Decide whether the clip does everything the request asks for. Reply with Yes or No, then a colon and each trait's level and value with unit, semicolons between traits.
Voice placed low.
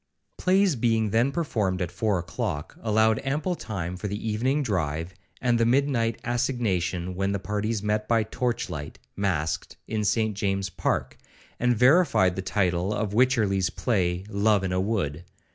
Yes: low, 105 Hz